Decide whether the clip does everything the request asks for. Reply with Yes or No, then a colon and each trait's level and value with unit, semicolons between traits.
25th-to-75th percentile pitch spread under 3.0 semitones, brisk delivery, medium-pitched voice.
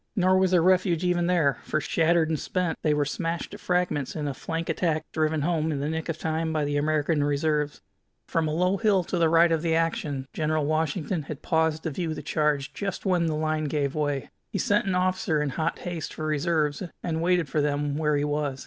Yes: narrow, 2.5 semitones; fast, 225 wpm; medium, 160 Hz